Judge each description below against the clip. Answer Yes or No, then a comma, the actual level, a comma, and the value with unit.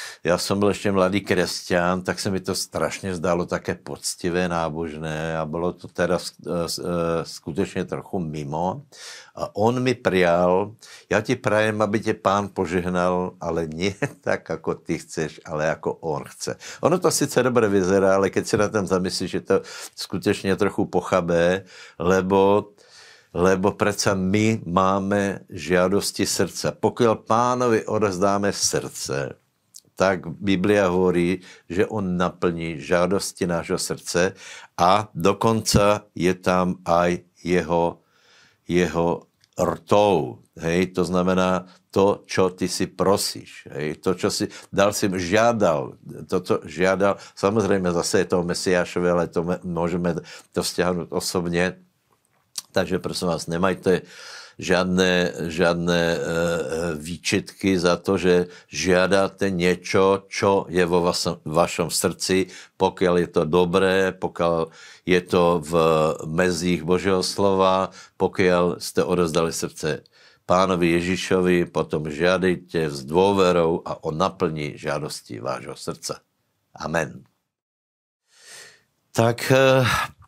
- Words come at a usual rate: Yes, average, 125 wpm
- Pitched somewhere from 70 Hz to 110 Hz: Yes, very low, 90 Hz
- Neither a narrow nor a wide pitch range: No, narrow, 2.2 semitones